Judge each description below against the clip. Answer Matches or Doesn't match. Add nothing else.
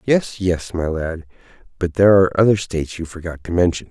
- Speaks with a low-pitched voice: Matches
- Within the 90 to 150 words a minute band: Doesn't match